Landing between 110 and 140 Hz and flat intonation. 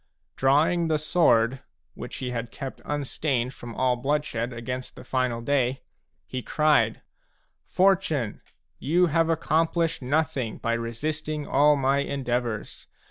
No: low, 135 Hz; average, 4.1 semitones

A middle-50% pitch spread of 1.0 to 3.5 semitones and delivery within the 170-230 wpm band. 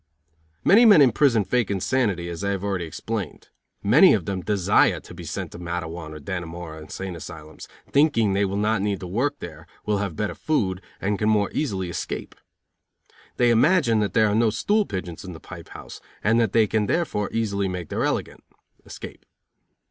No: average, 4.0 semitones; average, 190 wpm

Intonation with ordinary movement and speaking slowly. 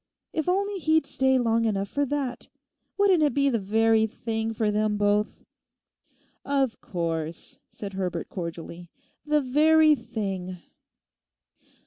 No: wide, 6.3 semitones; slow, 125 wpm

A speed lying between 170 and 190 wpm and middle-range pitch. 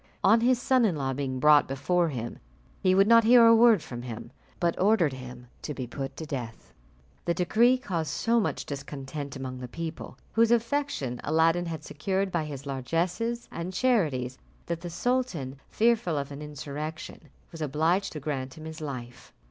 Yes: average, 180 wpm; medium, 160 Hz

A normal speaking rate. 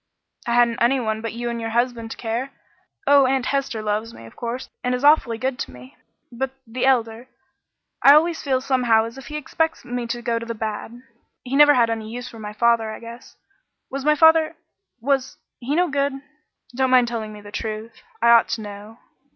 No: fast, 210 wpm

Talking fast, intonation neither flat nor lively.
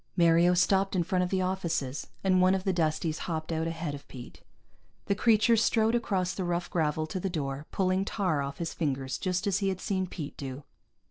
Yes: fast, 210 wpm; average, 3.4 semitones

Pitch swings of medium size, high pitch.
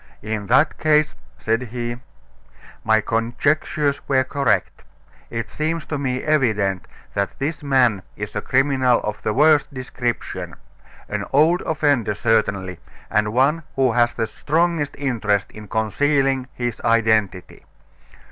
No: average, 4.6 semitones; low, 125 Hz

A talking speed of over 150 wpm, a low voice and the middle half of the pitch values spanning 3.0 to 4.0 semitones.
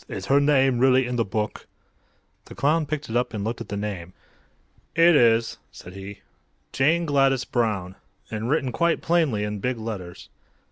No: average, 175 wpm; low, 120 Hz; average, 5.0 semitones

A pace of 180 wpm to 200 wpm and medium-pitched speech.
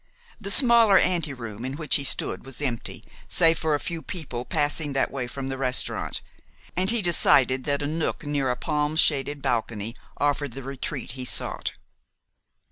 No: average, 170 wpm; medium, 145 Hz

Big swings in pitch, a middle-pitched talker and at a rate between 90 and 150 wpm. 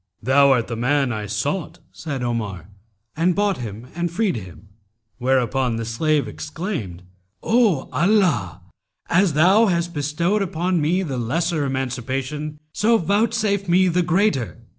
Yes: wide, 6.8 semitones; medium, 150 Hz; average, 140 wpm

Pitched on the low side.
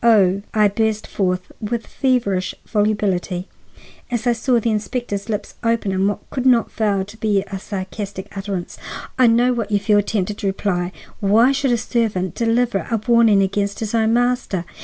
No: high, 210 Hz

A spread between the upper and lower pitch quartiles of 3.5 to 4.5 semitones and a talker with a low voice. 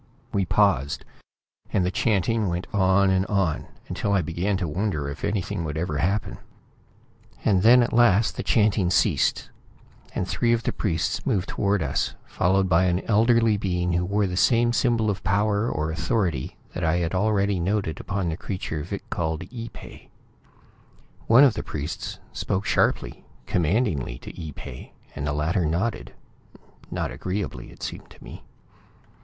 Yes: average, 3.8 semitones; very low, 95 Hz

